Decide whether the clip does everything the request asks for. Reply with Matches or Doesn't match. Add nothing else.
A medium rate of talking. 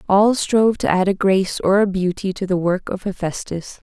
Doesn't match